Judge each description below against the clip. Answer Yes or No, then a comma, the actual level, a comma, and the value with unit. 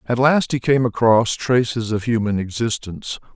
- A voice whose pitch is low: Yes, low, 115 Hz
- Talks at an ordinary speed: Yes, average, 160 wpm